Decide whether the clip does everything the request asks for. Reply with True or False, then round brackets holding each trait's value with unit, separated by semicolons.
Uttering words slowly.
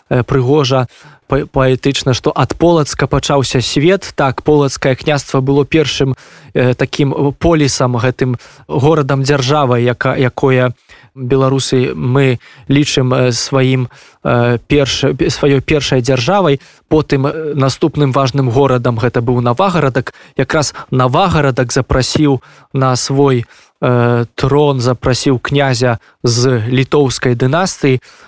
True (100 wpm)